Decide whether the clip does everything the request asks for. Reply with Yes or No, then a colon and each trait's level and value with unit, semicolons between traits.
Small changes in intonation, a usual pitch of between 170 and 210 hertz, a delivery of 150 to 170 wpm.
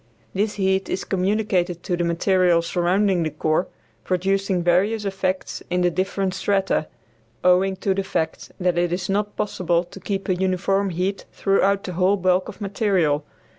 Yes: narrow, 1.8 semitones; medium, 185 Hz; average, 165 wpm